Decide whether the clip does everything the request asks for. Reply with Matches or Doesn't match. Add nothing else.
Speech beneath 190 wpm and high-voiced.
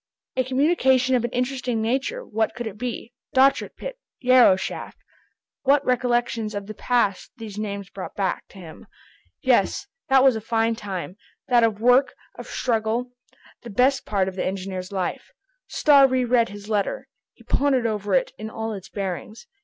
Matches